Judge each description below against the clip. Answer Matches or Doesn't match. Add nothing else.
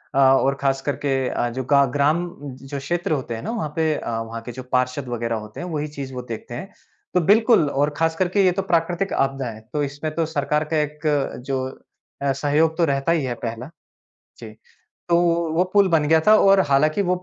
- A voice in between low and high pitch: Matches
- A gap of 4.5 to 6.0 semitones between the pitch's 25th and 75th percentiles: Doesn't match